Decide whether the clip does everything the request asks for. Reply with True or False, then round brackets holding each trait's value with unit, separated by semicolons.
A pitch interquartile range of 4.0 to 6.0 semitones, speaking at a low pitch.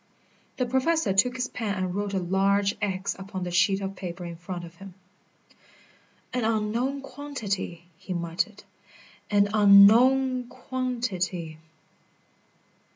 False (5.1 semitones; 200 Hz)